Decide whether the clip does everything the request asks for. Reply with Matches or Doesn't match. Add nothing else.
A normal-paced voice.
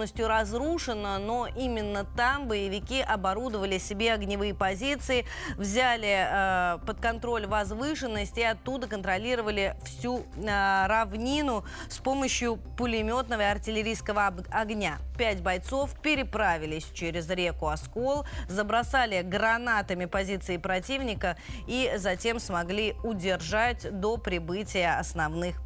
Doesn't match